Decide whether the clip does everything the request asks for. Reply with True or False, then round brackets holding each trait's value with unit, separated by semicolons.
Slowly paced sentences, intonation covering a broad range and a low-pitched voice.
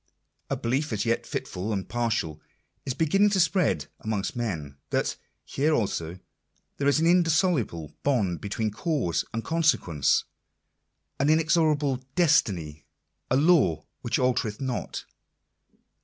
True (130 wpm; 8.3 semitones; 120 Hz)